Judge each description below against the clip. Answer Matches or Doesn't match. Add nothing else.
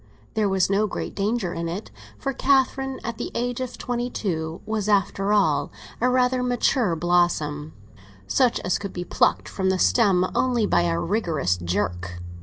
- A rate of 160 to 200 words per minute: Matches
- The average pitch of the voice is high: Matches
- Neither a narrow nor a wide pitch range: Doesn't match